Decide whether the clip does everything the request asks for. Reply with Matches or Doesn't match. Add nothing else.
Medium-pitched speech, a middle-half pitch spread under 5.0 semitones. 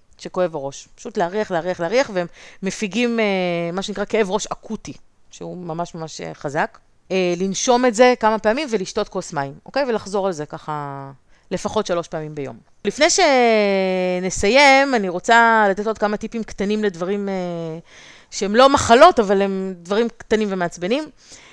Doesn't match